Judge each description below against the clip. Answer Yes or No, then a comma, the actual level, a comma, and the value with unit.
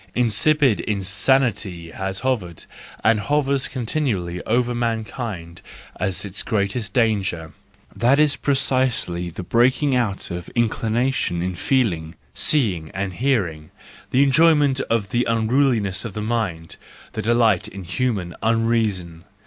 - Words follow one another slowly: Yes, slow, 125 wpm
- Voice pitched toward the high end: No, low, 110 Hz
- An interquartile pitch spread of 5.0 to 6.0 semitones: Yes, average, 5.3 semitones